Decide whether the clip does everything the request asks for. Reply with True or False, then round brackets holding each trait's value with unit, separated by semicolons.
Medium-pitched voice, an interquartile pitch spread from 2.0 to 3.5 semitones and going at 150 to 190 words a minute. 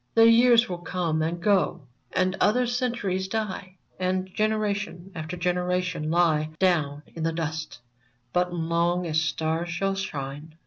False (180 Hz; 3.1 semitones; 140 wpm)